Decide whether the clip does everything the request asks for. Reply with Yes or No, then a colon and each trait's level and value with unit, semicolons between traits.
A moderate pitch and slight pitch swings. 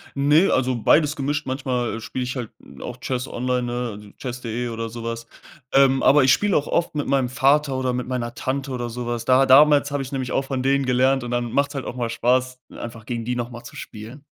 No: low, 130 Hz; narrow, 2.2 semitones